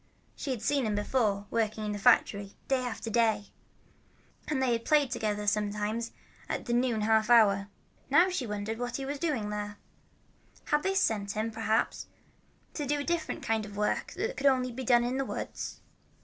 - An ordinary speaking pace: Yes, average, 190 wpm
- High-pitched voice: Yes, high, 230 Hz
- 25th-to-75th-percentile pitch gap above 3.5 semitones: Yes, average, 4.1 semitones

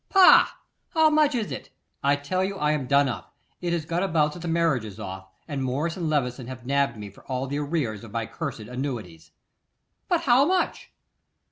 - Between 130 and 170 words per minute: No, fast, 205 wpm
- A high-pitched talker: No, medium, 145 Hz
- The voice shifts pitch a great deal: Yes, wide, 5.7 semitones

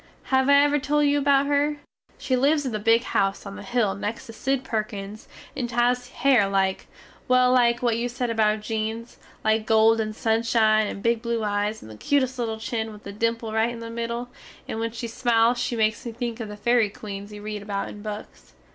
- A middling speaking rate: No, fast, 220 wpm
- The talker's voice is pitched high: Yes, high, 230 Hz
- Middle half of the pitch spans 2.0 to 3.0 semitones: Yes, narrow, 2.4 semitones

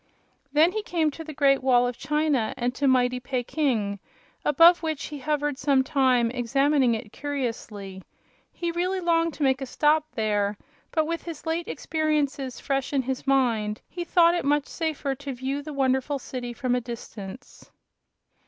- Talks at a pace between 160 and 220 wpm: Yes, average, 170 wpm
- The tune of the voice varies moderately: Yes, average, 3.8 semitones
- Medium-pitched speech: No, very high, 275 Hz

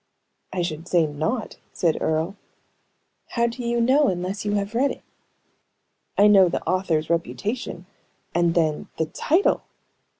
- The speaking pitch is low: No, medium, 185 Hz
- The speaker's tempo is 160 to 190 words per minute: No, average, 140 wpm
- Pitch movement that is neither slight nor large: No, wide, 5.7 semitones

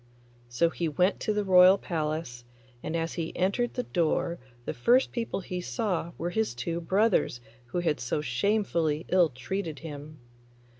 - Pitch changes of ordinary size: Yes, average, 4.1 semitones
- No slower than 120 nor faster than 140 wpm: No, average, 160 wpm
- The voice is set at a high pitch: No, medium, 170 Hz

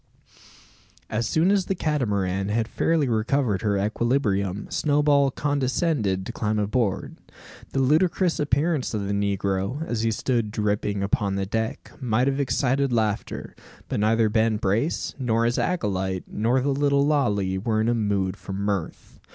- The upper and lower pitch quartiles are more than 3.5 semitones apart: Yes, wide, 5.4 semitones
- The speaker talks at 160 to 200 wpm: No, average, 150 wpm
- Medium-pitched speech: No, low, 115 Hz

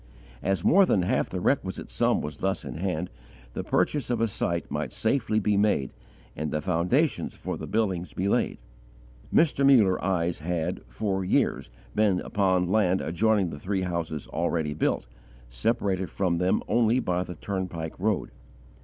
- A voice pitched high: No, very low, 95 Hz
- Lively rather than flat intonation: No, average, 3.9 semitones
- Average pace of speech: Yes, average, 160 wpm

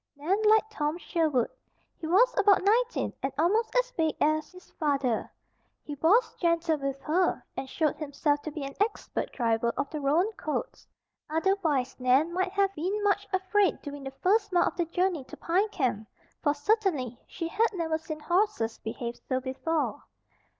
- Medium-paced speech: Yes, average, 170 wpm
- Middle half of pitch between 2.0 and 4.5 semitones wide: No, wide, 5.5 semitones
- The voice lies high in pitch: Yes, very high, 325 Hz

